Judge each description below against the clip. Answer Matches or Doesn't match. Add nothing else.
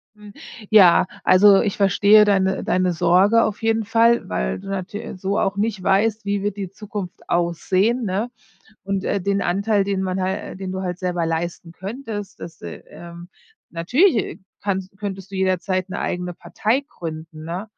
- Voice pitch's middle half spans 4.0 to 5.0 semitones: Doesn't match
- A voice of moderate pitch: Doesn't match